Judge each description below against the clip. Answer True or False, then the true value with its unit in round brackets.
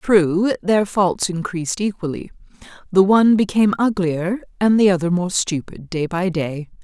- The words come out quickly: False (150 wpm)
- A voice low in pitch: False (185 Hz)